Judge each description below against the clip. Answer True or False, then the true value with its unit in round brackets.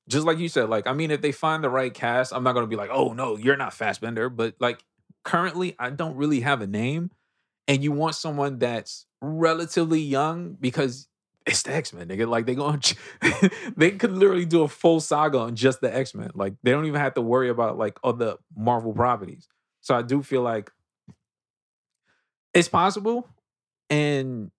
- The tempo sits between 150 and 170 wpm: False (200 wpm)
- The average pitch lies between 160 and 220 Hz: False (140 Hz)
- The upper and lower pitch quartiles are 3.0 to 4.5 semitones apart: False (5.0 semitones)